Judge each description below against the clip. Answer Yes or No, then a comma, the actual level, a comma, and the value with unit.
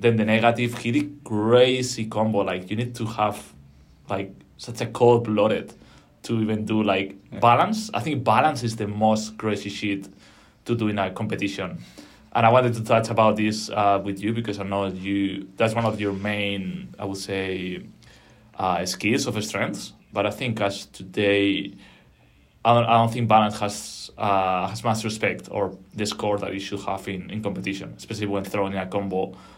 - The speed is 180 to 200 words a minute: Yes, average, 185 wpm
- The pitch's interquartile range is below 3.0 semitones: Yes, narrow, 2.5 semitones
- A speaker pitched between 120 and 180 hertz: No, low, 105 Hz